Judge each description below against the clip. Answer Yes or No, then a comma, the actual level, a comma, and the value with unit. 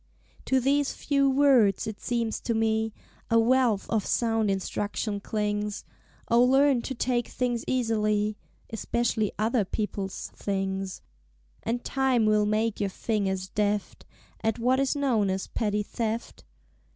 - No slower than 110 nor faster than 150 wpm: Yes, average, 140 wpm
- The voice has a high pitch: Yes, high, 220 Hz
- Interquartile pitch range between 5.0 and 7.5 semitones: No, average, 2.8 semitones